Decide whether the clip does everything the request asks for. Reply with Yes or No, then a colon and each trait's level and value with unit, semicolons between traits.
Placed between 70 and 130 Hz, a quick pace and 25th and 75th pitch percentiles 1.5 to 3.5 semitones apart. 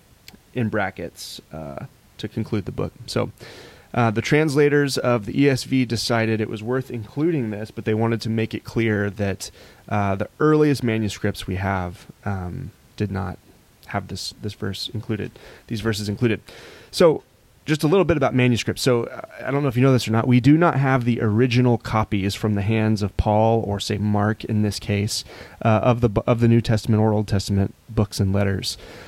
No: low, 110 Hz; average, 195 wpm; average, 3.1 semitones